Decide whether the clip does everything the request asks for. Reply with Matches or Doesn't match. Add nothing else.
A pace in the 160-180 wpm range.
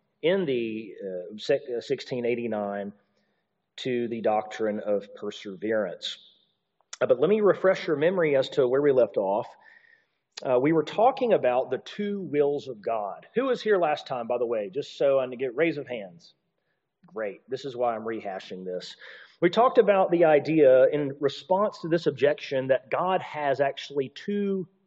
Matches